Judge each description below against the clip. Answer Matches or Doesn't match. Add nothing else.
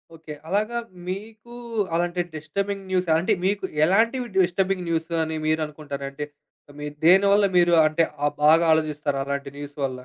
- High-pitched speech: Doesn't match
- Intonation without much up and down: Doesn't match